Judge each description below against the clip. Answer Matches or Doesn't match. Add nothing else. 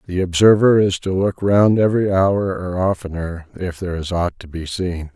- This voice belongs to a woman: Doesn't match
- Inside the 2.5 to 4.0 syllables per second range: Doesn't match